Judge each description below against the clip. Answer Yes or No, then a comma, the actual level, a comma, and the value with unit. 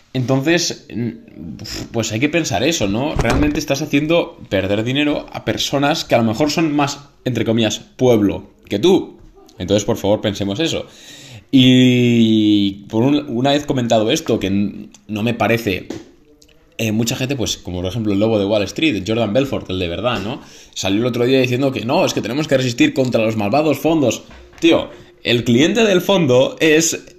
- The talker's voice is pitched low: Yes, low, 120 Hz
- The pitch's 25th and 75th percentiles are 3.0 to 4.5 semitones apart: No, average, 5.2 semitones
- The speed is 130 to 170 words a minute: No, average, 180 wpm